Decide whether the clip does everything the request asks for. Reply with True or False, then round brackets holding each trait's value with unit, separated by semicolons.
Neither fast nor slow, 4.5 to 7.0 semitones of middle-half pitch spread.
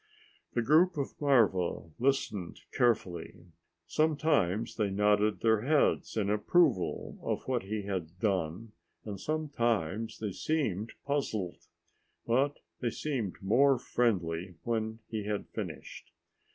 False (115 wpm; 5.4 semitones)